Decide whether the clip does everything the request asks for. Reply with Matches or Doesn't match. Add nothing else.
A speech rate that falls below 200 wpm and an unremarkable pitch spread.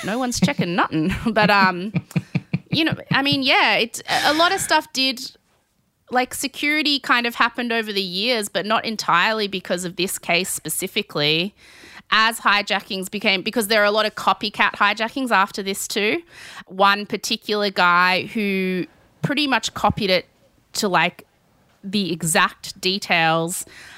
Matches